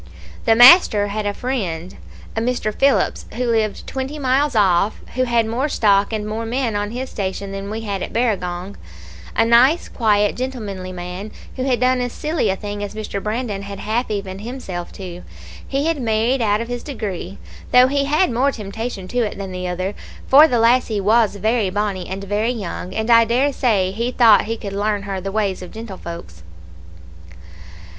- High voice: Yes, high, 215 Hz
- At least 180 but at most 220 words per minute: Yes, average, 190 wpm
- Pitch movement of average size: Yes, average, 3.8 semitones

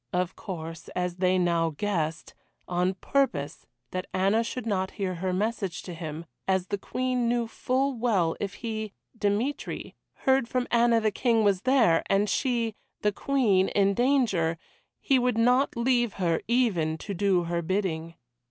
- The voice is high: Yes, high, 200 Hz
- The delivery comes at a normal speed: Yes, average, 160 wpm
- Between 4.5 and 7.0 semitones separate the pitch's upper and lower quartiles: Yes, average, 4.9 semitones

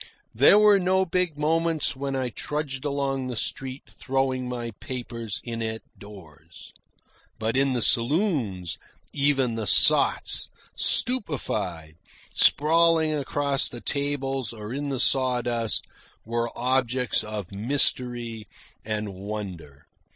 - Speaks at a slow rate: Yes, slow, 115 wpm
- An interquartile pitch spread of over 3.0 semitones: Yes, average, 4.3 semitones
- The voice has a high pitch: No, low, 130 Hz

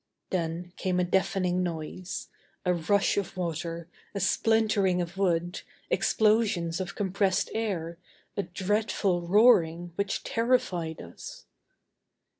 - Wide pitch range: No, average, 2.9 semitones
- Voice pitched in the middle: Yes, medium, 180 Hz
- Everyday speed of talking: No, slow, 110 wpm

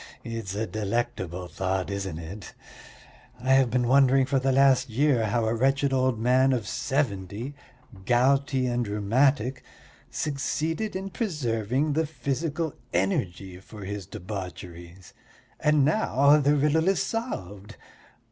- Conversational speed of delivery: No, slow, 130 wpm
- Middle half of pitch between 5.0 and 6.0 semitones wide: Yes, wide, 5.5 semitones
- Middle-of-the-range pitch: No, low, 125 Hz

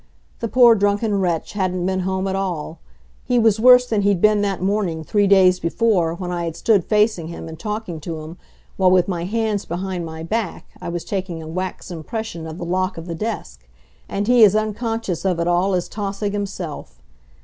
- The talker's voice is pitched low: No, high, 190 Hz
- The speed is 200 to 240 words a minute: Yes, fast, 205 wpm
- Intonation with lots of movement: No, average, 3.6 semitones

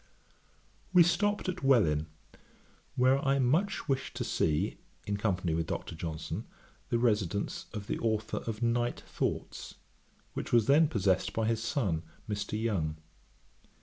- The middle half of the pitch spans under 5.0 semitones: No, wide, 5.6 semitones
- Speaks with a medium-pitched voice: No, low, 115 Hz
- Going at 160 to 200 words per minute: No, average, 140 wpm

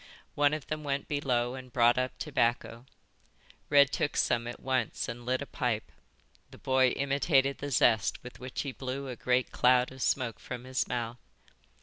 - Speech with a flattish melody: Yes, narrow, 2.3 semitones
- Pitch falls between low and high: No, low, 130 Hz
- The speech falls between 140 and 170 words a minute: No, average, 180 wpm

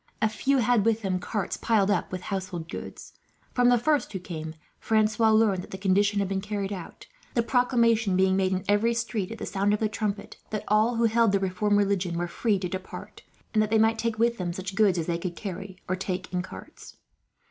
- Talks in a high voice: Yes, high, 205 Hz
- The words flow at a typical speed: No, fast, 225 wpm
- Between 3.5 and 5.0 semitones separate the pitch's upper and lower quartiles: No, average, 3.0 semitones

